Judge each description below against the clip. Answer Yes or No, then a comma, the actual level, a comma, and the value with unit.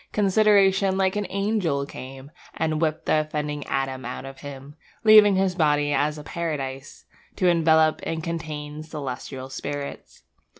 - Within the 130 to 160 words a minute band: Yes, average, 140 wpm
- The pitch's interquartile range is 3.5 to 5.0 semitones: Yes, average, 4.7 semitones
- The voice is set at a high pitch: No, medium, 155 Hz